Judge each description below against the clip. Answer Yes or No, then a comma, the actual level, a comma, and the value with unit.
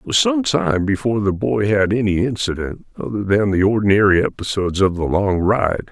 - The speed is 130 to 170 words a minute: No, average, 195 wpm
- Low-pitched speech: Yes, low, 105 Hz